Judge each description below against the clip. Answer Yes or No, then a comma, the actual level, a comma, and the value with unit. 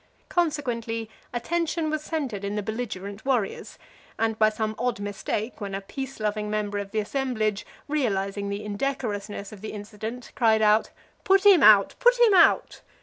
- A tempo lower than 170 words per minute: Yes, average, 160 wpm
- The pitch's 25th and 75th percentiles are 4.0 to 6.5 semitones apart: Yes, average, 4.6 semitones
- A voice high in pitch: Yes, high, 220 Hz